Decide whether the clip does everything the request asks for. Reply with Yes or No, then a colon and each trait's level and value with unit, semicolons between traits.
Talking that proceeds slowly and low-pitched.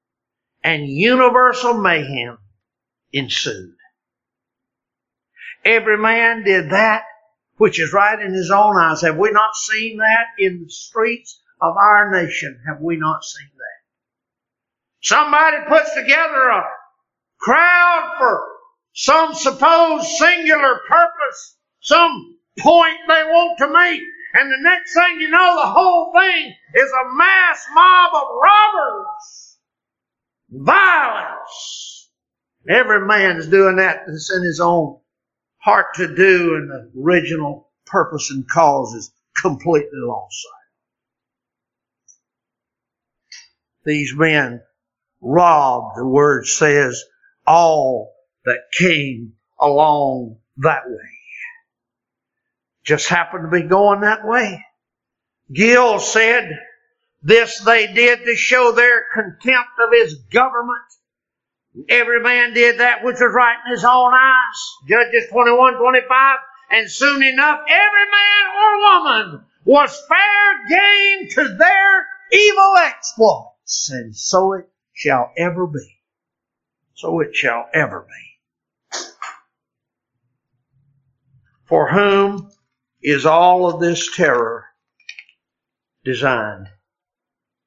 No: slow, 115 wpm; high, 230 Hz